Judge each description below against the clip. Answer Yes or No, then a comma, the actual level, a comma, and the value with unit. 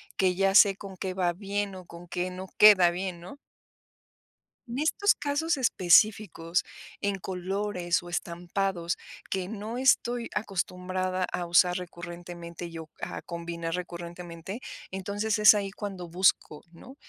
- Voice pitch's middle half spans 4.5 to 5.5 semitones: No, average, 2.7 semitones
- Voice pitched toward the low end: No, medium, 185 Hz